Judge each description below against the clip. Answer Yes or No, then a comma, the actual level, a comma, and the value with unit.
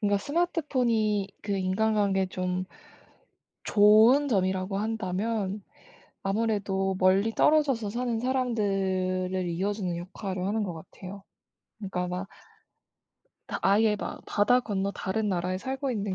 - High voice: Yes, high, 200 Hz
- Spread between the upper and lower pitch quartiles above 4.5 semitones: No, average, 3.0 semitones